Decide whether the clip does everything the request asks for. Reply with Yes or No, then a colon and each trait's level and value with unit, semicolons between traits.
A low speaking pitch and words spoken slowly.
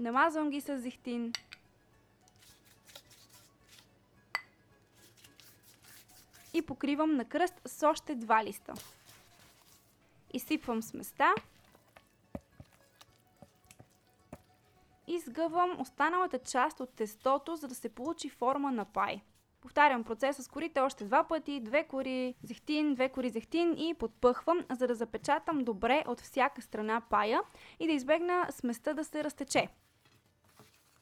No: very high, 260 Hz; slow, 110 wpm